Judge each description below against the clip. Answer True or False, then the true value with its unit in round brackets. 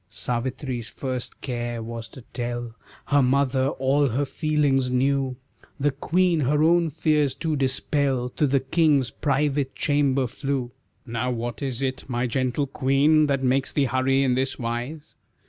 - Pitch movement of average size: False (2.3 semitones)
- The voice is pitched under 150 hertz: True (135 Hz)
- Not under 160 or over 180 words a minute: False (150 wpm)